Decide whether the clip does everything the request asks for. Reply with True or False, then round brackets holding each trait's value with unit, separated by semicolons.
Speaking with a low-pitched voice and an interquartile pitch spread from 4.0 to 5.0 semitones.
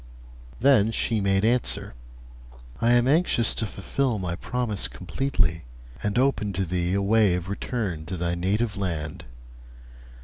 True (100 Hz; 4.7 semitones)